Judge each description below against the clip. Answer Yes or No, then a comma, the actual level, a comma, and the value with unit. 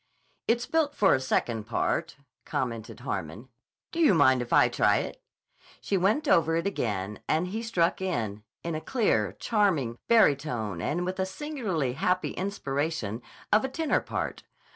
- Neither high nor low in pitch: Yes, medium, 165 Hz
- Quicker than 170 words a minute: No, average, 165 wpm